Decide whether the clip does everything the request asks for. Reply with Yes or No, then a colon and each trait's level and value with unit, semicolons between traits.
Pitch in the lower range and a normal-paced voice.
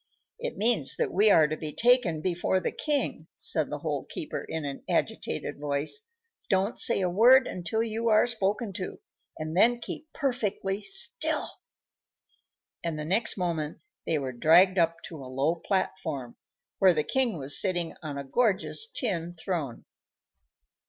No: medium, 185 Hz; average, 160 wpm